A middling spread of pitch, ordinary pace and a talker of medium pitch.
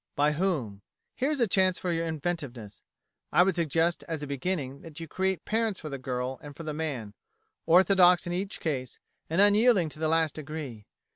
Yes: average, 4.6 semitones; average, 195 wpm; medium, 160 Hz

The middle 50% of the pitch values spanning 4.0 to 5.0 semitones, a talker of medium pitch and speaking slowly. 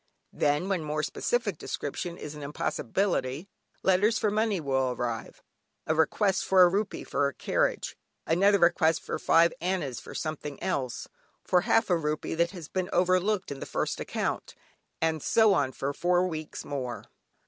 No: average, 4.6 semitones; medium, 170 Hz; average, 160 wpm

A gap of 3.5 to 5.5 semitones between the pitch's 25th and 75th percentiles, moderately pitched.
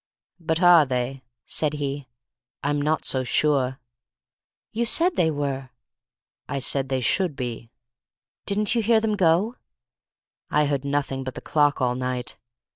Yes: average, 4.2 semitones; medium, 145 Hz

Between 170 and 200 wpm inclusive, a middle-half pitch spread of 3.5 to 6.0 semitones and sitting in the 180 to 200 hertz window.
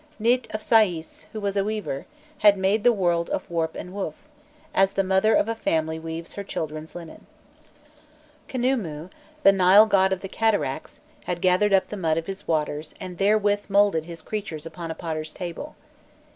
Yes: average, 180 wpm; average, 4.0 semitones; high, 190 Hz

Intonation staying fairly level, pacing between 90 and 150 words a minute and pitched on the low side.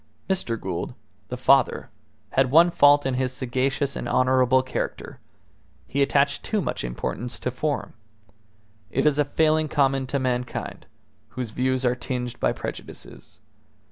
Yes: narrow, 2.3 semitones; average, 140 wpm; low, 130 Hz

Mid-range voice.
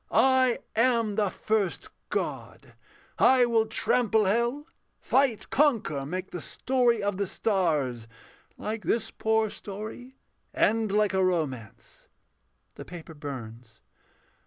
No: high, 210 Hz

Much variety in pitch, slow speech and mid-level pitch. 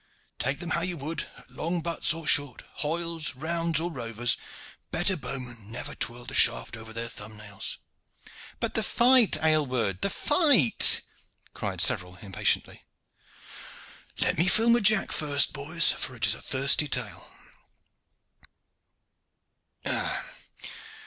Yes: wide, 6.3 semitones; slow, 130 wpm; medium, 145 Hz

